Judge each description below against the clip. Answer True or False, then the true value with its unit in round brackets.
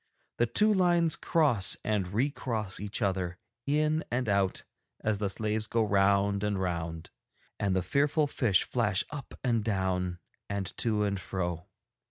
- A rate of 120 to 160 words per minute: True (155 wpm)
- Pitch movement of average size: True (4.3 semitones)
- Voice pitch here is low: True (105 Hz)